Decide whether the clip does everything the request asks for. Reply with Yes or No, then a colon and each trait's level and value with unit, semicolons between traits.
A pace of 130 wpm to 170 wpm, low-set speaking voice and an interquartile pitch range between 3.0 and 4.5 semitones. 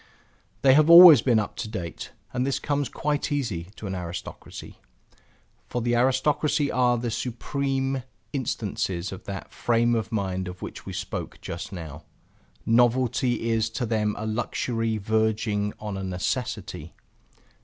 Yes: average, 145 wpm; low, 115 Hz; average, 4.0 semitones